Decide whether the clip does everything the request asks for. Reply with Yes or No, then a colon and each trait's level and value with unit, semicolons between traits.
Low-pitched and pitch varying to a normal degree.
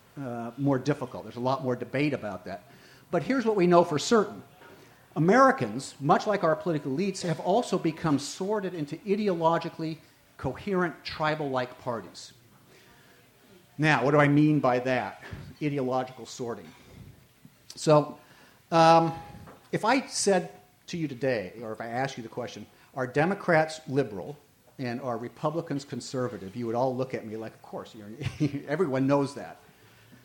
No: medium, 145 Hz; average, 4.8 semitones